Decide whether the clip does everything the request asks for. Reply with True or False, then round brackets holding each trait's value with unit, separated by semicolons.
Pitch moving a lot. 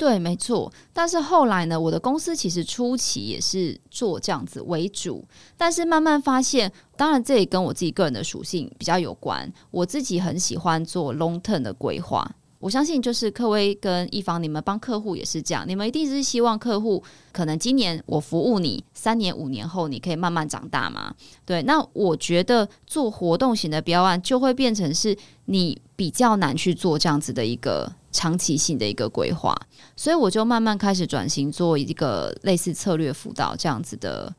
True (6.3 semitones)